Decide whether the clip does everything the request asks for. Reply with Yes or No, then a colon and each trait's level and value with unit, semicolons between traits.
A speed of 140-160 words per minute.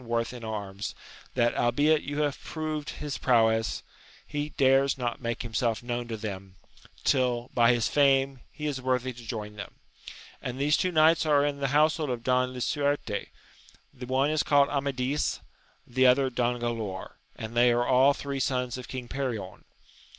No: average, 170 wpm